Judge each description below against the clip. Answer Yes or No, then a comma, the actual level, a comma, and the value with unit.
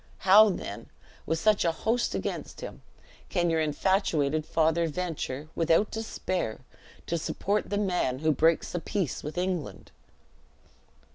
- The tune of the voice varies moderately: Yes, average, 3.7 semitones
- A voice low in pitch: No, medium, 170 Hz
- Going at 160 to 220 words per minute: No, slow, 135 wpm